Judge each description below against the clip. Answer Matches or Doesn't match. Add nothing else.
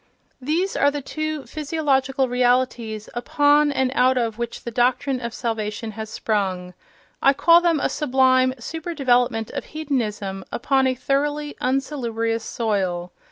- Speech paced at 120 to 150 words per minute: Matches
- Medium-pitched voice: Doesn't match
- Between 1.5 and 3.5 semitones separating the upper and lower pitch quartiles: Doesn't match